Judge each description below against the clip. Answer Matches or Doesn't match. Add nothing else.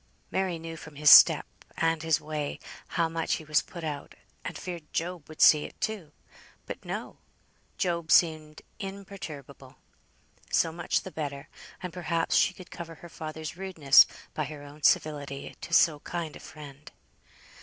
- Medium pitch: Matches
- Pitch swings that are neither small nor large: Doesn't match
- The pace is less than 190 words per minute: Matches